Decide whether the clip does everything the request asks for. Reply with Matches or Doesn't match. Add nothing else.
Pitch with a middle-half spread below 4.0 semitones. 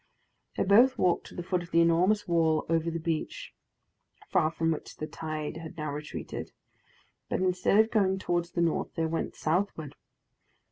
Matches